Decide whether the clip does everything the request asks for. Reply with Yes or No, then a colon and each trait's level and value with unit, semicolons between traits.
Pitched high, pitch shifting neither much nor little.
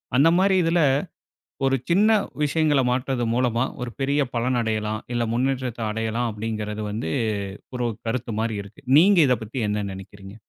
No: low, 120 Hz; average, 3.7 semitones